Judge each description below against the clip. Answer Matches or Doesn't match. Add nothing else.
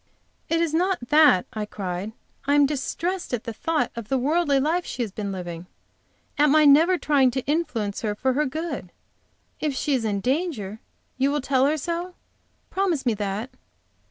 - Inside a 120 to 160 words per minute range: Doesn't match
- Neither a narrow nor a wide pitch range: Doesn't match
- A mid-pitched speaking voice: Doesn't match